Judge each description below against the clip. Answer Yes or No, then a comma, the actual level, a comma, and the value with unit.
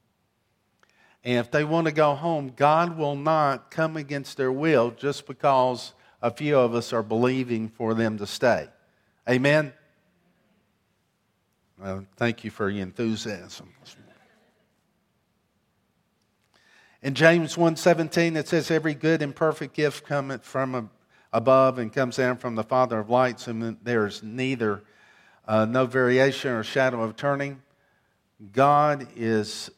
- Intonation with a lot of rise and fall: No, average, 4.6 semitones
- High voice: No, low, 130 Hz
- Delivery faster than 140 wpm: No, slow, 135 wpm